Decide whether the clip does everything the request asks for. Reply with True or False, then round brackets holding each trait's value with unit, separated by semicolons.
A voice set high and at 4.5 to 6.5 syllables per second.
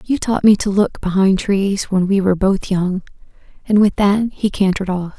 True (195 Hz; 5.0 syllables/s)